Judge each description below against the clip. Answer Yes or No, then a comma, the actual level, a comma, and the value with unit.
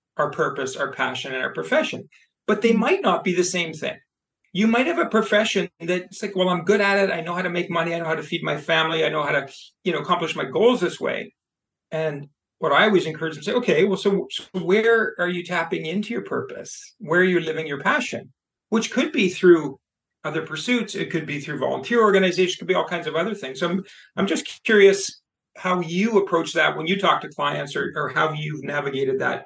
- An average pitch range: Yes, average, 3.7 semitones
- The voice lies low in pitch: No, medium, 180 Hz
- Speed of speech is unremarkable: No, fast, 230 wpm